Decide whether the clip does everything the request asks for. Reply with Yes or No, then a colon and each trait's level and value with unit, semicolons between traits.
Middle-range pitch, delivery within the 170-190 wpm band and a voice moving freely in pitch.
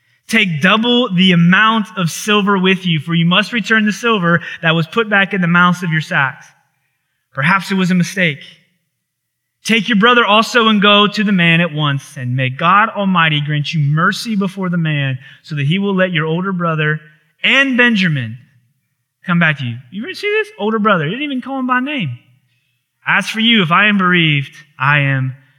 No: medium, 175 Hz; average, 200 wpm; wide, 6.0 semitones